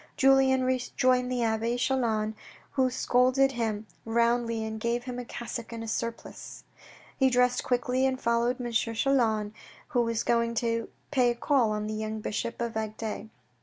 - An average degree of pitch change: No, narrow, 2.1 semitones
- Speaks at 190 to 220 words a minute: No, average, 165 wpm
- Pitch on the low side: No, high, 235 Hz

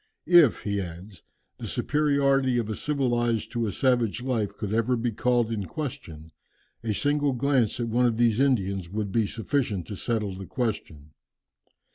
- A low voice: Yes, low, 115 Hz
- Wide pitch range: No, average, 4.1 semitones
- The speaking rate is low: No, average, 165 wpm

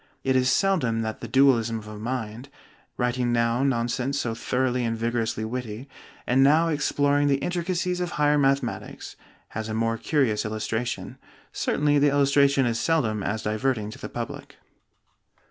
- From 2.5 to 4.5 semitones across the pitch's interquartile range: Yes, average, 3.8 semitones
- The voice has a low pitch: Yes, low, 125 Hz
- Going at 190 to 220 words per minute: No, average, 155 wpm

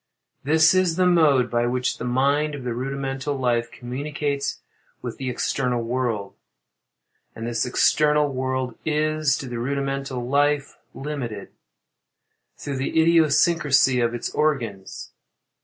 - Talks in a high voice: No, low, 135 Hz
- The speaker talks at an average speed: No, slow, 125 wpm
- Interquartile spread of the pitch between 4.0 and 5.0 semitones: No, average, 3.2 semitones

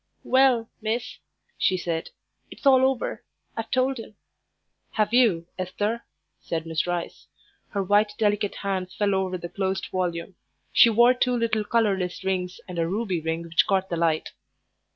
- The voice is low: No, high, 195 Hz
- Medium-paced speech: Yes, average, 155 wpm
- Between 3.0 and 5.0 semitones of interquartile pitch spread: Yes, average, 4.3 semitones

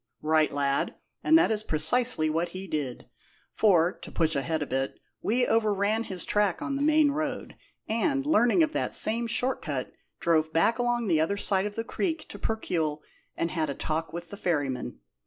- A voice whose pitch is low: No, high, 190 Hz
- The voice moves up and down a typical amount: No, wide, 7.1 semitones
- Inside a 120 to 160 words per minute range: No, average, 190 wpm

